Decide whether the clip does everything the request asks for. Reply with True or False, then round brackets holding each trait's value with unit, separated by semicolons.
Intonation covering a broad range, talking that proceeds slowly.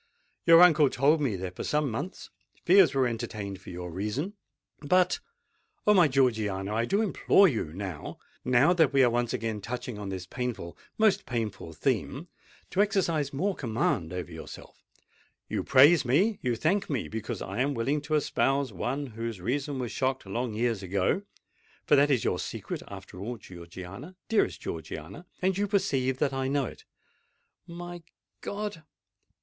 False (7.4 semitones; 150 wpm)